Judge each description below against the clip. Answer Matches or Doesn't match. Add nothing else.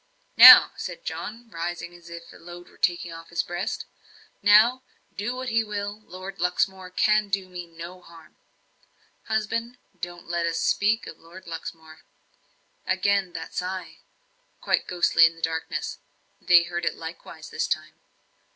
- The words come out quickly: Doesn't match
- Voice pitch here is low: Doesn't match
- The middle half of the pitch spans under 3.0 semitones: Doesn't match